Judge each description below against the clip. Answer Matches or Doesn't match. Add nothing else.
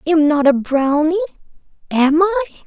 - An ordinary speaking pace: Matches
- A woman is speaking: Matches